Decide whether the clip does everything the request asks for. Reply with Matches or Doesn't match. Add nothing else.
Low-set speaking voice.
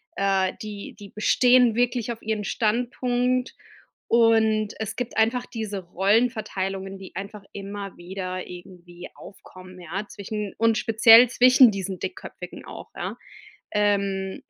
Doesn't match